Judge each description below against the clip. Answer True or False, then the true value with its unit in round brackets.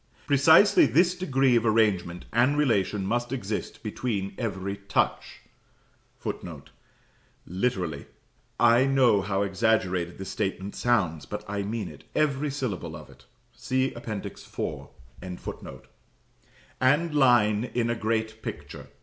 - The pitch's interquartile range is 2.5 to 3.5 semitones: False (5.0 semitones)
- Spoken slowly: True (120 wpm)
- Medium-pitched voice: False (110 Hz)